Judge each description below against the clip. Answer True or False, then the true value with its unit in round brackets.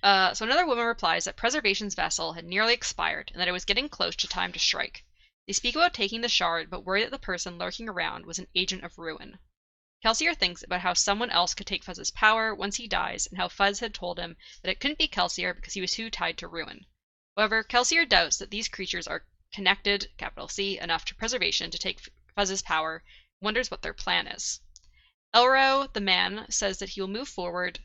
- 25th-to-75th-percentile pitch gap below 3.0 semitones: False (4.1 semitones)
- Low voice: False (200 Hz)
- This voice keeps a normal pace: False (220 wpm)